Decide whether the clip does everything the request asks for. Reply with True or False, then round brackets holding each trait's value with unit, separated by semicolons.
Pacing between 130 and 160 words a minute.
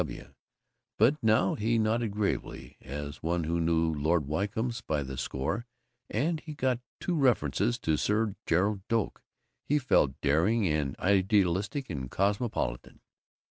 True (145 wpm)